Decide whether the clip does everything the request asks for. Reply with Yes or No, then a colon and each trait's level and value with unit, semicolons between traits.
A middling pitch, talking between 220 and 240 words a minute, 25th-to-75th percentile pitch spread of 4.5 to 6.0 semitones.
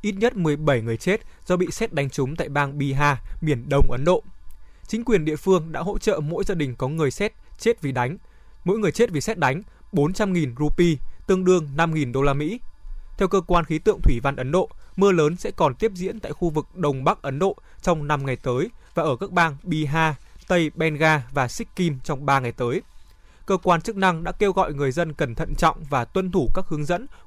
Yes: medium, 160 Hz; average, 230 wpm; average, 4.8 semitones